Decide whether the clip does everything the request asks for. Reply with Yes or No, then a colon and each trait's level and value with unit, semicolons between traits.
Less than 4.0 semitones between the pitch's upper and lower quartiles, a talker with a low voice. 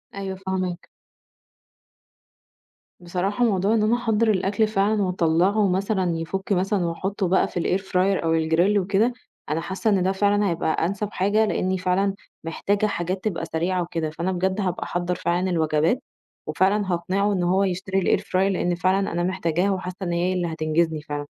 No: narrow, 2.4 semitones; medium, 185 Hz